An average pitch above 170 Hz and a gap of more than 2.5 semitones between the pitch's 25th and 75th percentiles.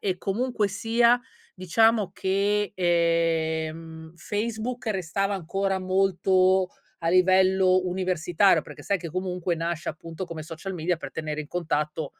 Yes: medium, 185 Hz; average, 2.9 semitones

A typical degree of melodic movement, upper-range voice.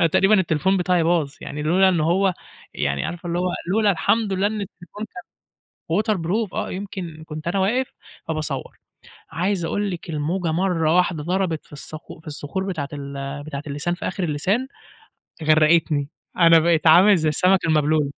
No: average, 3.6 semitones; medium, 170 Hz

